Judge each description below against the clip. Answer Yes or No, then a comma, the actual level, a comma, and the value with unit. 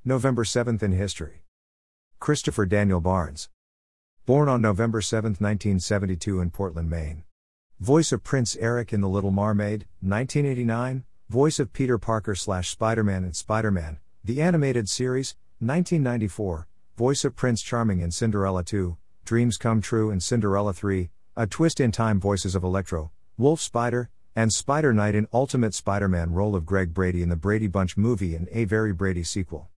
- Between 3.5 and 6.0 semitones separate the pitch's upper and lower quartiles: Yes, average, 4.4 semitones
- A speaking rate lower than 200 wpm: Yes, average, 160 wpm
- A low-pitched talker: Yes, low, 105 Hz